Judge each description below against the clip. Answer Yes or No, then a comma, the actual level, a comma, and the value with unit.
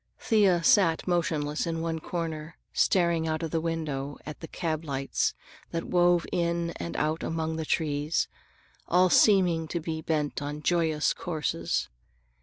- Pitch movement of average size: No, narrow, 2.0 semitones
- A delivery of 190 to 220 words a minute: No, average, 150 wpm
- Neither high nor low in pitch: Yes, medium, 160 Hz